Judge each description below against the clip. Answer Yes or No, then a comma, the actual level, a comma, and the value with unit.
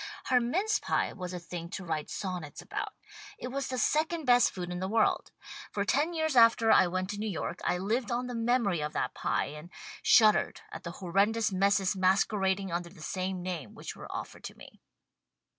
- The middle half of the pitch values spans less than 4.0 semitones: No, average, 5.0 semitones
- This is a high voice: Yes, high, 195 Hz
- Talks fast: Yes, fast, 210 wpm